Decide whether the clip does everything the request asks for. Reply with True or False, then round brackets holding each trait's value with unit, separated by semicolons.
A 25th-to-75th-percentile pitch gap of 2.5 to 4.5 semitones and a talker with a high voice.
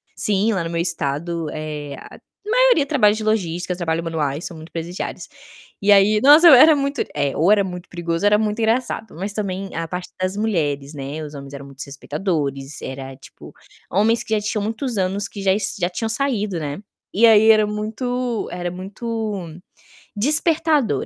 False (5.4 semitones; 195 Hz)